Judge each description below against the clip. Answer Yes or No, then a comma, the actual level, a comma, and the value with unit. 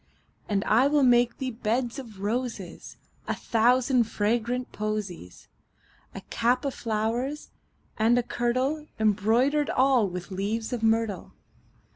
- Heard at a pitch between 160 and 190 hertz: No, high, 230 Hz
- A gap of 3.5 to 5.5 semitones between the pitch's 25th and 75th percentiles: No, average, 3.0 semitones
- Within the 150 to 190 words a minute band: No, slow, 135 wpm